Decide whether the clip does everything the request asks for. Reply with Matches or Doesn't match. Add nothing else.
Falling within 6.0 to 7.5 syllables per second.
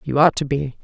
Doesn't match